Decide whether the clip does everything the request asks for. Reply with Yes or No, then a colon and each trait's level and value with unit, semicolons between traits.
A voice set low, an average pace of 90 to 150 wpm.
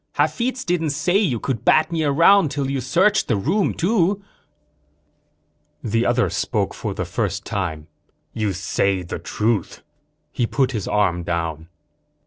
Yes: low, 130 Hz; average, 145 wpm